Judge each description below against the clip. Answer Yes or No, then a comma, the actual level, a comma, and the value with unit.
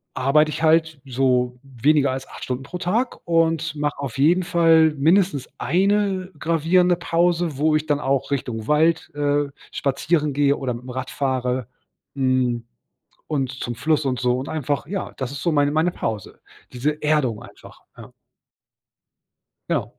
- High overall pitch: No, medium, 145 Hz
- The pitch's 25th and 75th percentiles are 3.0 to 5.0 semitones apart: Yes, average, 3.9 semitones